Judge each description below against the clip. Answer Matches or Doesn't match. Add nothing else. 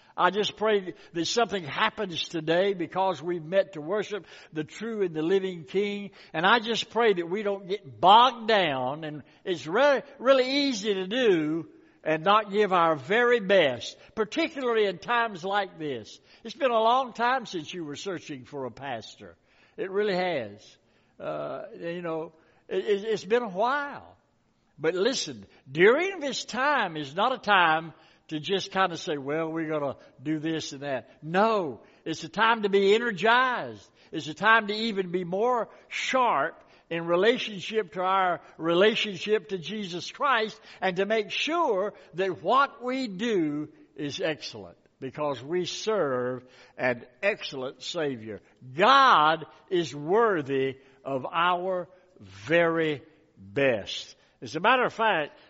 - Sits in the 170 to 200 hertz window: Matches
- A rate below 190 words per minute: Matches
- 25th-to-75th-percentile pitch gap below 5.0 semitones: Doesn't match